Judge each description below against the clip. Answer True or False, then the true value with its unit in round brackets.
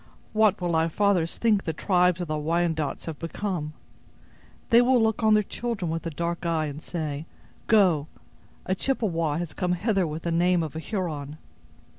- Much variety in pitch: False (3.9 semitones)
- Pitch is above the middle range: False (170 Hz)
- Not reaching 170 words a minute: False (180 wpm)